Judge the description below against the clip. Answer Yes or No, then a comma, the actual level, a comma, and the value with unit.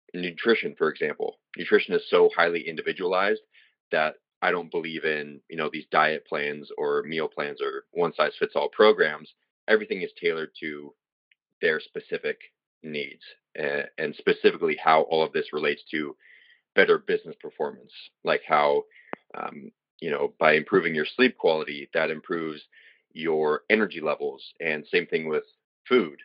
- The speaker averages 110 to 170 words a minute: Yes, average, 150 wpm